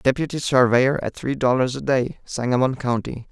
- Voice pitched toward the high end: No, low, 130 Hz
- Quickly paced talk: No, average, 165 wpm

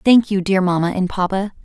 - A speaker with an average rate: No, fast, 220 wpm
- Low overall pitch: No, high, 190 Hz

